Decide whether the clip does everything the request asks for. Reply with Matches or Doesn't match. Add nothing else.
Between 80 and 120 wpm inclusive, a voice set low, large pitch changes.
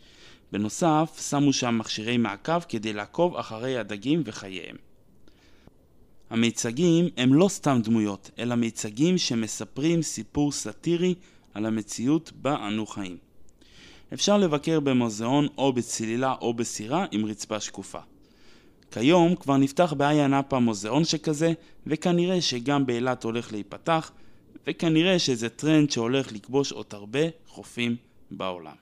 Matches